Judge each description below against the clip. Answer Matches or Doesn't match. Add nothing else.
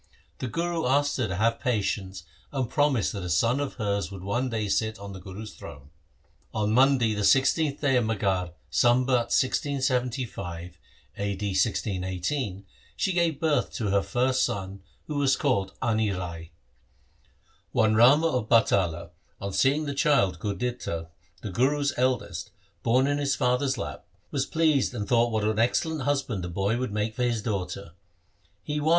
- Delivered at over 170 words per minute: Doesn't match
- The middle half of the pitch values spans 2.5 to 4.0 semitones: Doesn't match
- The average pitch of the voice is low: Matches